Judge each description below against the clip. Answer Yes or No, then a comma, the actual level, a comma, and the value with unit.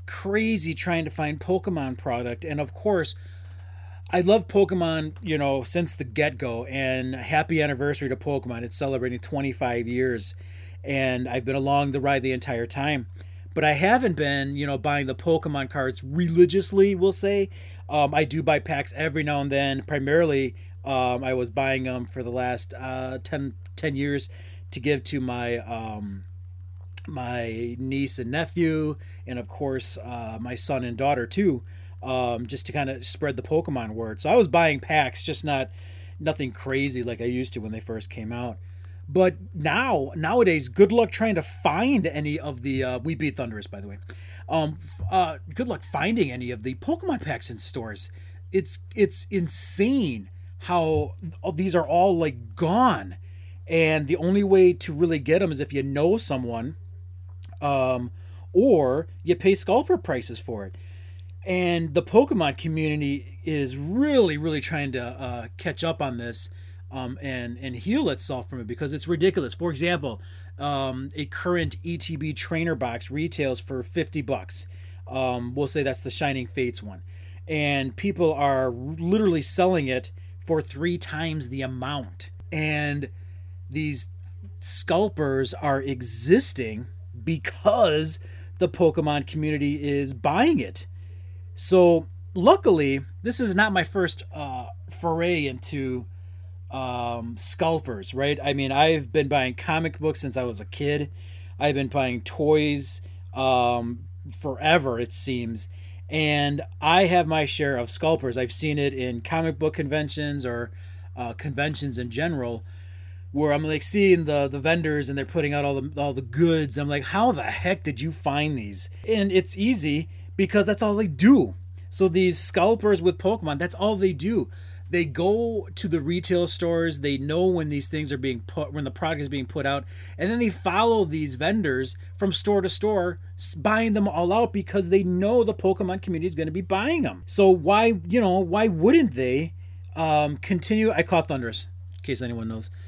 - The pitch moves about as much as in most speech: No, wide, 8.5 semitones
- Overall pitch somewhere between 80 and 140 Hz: Yes, low, 135 Hz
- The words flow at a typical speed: Yes, average, 170 wpm